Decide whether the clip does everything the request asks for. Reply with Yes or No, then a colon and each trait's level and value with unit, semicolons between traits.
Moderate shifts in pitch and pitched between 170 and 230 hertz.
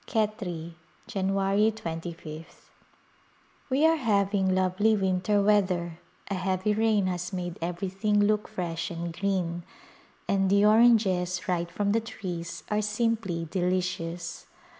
Yes: average, 3.1 semitones; high, 190 Hz